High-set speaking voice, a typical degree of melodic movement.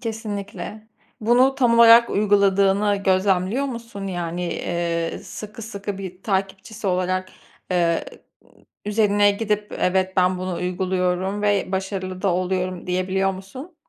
No: high, 195 Hz; narrow, 2.3 semitones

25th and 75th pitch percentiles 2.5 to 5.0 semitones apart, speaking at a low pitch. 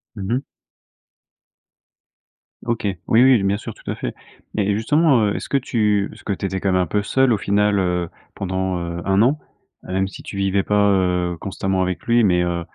Yes: average, 2.8 semitones; low, 100 Hz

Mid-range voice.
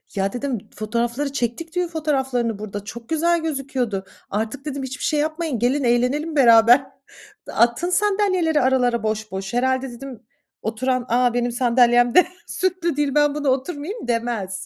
No: very high, 260 Hz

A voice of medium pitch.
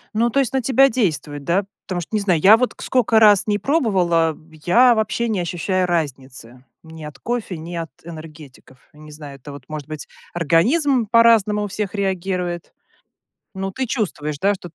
Yes: medium, 180 Hz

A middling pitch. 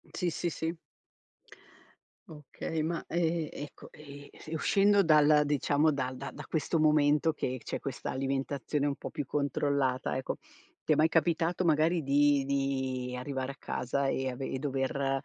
Yes: medium, 145 Hz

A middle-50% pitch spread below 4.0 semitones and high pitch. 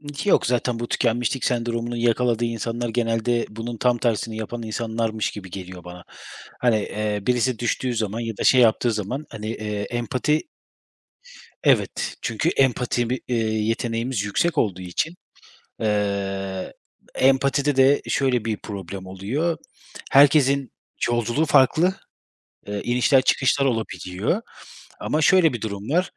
No: average, 3.4 semitones; low, 120 Hz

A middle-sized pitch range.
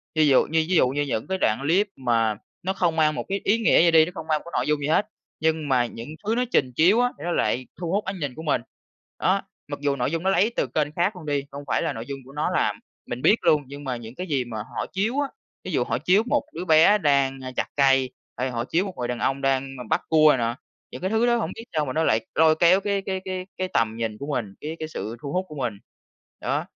No: wide, 6.0 semitones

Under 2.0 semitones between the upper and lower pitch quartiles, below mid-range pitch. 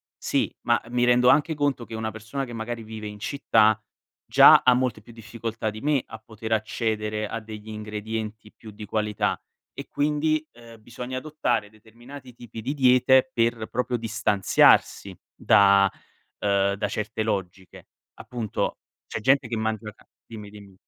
No: narrow, 2.4 semitones; low, 110 Hz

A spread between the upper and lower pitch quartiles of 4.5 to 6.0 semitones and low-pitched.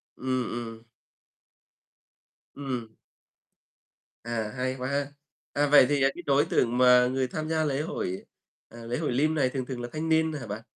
No: average, 3.3 semitones; low, 130 Hz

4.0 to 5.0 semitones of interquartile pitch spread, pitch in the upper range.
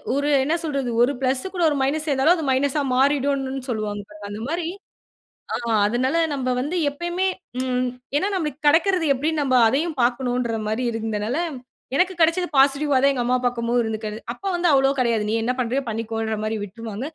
Yes: average, 4.3 semitones; very high, 265 Hz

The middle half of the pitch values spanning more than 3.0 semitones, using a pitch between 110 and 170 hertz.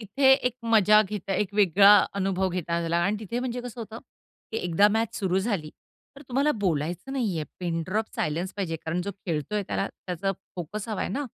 No: average, 4.1 semitones; high, 195 Hz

